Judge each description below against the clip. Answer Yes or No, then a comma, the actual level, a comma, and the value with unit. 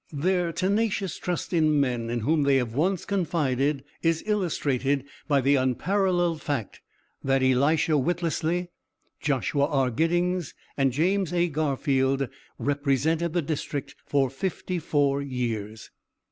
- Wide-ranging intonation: No, average, 4.4 semitones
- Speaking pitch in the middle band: Yes, medium, 145 Hz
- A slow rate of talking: Yes, slow, 125 wpm